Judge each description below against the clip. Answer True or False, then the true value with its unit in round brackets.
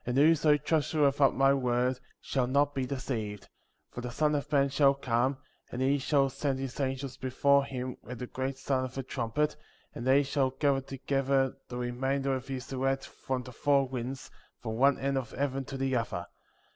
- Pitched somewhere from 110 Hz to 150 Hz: True (135 Hz)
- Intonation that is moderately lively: False (1.6 semitones)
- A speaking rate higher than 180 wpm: True (195 wpm)